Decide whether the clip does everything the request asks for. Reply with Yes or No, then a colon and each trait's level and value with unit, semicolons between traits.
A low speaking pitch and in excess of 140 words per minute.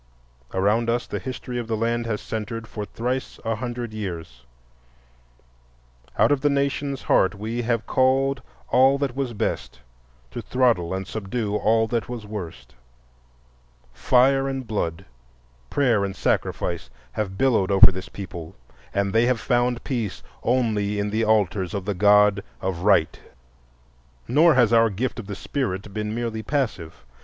Yes: low, 110 Hz; average, 150 wpm